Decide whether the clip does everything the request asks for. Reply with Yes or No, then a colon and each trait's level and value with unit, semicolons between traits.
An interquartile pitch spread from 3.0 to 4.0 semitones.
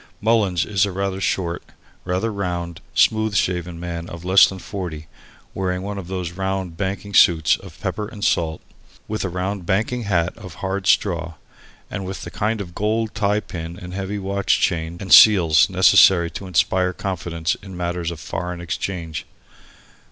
No: narrow, 2.5 semitones